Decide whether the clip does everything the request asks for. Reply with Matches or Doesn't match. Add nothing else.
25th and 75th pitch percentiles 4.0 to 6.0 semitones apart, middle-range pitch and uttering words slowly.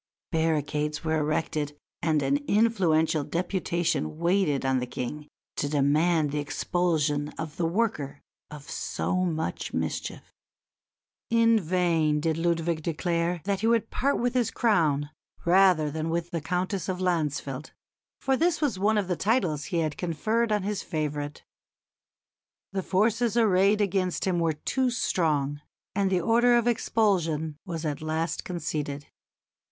Doesn't match